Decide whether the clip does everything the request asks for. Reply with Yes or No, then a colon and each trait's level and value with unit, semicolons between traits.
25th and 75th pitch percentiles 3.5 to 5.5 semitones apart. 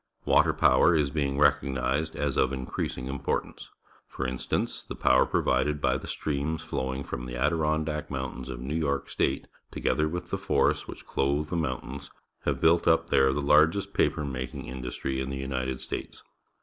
No: average, 2.7 semitones